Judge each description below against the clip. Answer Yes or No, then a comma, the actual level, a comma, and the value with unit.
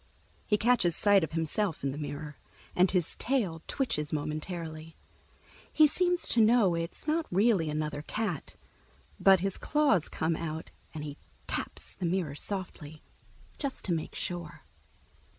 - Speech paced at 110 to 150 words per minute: Yes, average, 145 wpm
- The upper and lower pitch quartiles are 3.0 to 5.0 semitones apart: No, wide, 5.4 semitones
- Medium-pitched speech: Yes, medium, 175 Hz